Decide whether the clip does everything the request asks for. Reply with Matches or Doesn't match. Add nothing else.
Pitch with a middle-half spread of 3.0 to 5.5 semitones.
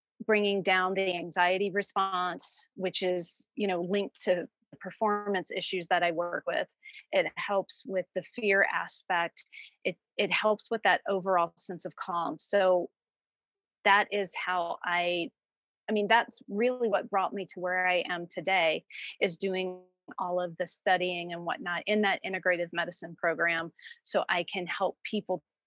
Doesn't match